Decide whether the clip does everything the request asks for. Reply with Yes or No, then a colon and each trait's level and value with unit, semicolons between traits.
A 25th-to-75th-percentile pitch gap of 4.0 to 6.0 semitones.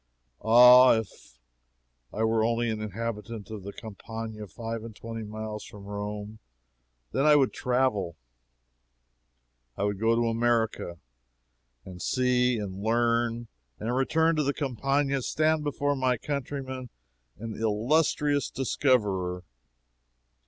No: average, 3.4 semitones